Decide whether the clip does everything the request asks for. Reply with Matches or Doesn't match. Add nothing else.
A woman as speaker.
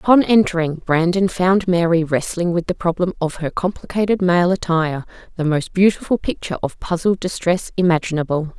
Matches